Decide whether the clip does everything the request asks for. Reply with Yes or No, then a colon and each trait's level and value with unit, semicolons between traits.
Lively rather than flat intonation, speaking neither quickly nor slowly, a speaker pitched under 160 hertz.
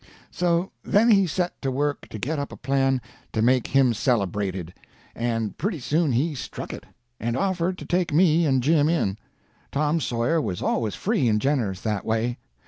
Yes: wide, 6.3 semitones; average, 180 wpm; low, 135 Hz